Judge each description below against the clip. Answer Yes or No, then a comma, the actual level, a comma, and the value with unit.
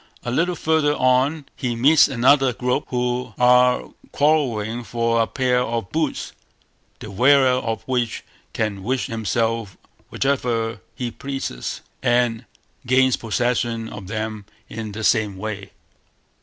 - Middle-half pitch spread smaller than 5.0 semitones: Yes, narrow, 2.6 semitones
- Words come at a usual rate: No, slow, 130 wpm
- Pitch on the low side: Yes, low, 120 Hz